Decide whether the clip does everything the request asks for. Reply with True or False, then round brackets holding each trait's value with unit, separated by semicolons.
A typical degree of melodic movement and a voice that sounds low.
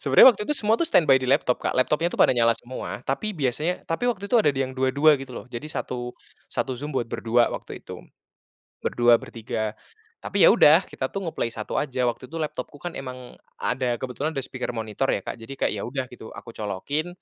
True (4.2 semitones; 130 Hz)